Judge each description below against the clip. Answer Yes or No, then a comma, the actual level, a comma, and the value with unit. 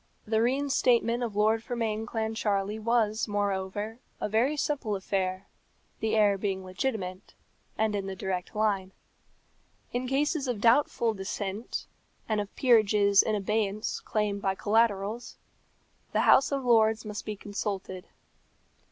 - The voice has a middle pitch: No, high, 215 Hz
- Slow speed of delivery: Yes, slow, 130 wpm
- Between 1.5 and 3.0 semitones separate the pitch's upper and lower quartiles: Yes, narrow, 2.5 semitones